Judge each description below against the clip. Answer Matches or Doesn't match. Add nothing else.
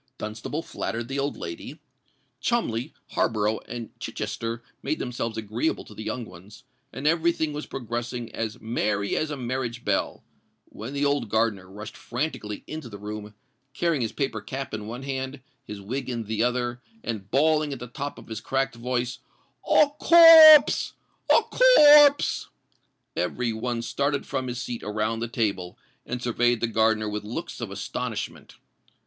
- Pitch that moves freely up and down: Doesn't match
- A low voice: Matches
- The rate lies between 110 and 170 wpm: Matches